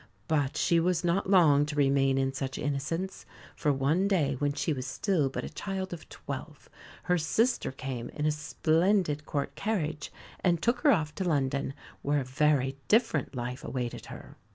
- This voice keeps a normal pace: Yes, average, 175 wpm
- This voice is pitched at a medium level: Yes, medium, 150 Hz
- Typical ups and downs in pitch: Yes, average, 4.6 semitones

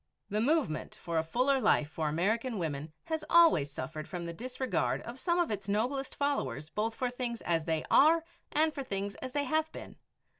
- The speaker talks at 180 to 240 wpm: Yes, average, 195 wpm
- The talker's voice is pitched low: No, high, 230 Hz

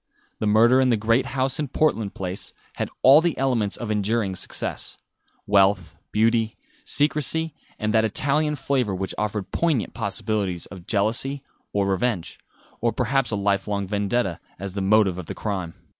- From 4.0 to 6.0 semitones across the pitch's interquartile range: Yes, average, 4.6 semitones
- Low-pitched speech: Yes, low, 110 Hz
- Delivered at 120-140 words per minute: No, average, 160 wpm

